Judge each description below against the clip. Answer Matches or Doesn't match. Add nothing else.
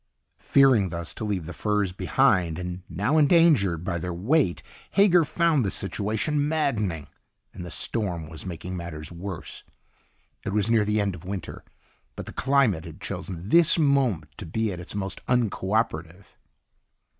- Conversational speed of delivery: Matches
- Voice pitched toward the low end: Matches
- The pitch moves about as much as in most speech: Doesn't match